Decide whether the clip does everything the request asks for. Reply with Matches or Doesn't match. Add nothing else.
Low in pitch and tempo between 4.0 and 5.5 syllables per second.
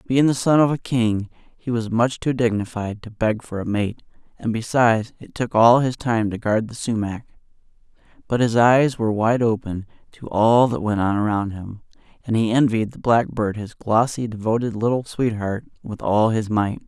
Matches